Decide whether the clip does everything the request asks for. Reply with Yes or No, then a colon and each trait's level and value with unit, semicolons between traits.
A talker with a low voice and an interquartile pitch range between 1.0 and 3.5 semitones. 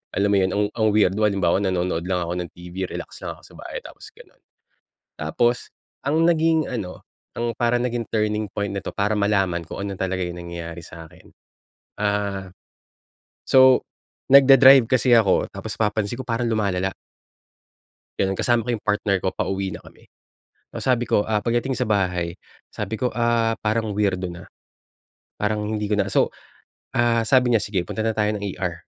No: low, 105 Hz; average, 3.9 semitones